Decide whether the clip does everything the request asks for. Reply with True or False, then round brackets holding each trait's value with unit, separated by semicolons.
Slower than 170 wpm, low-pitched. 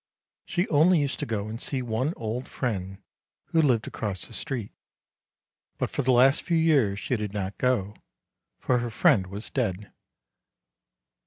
True (160 wpm; 120 Hz)